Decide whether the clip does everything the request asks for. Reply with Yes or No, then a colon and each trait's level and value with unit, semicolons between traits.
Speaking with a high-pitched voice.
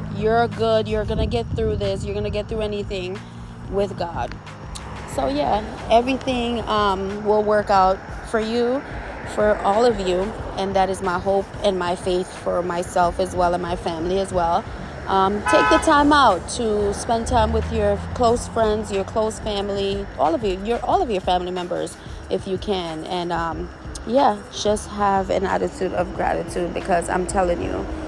Yes: high, 195 Hz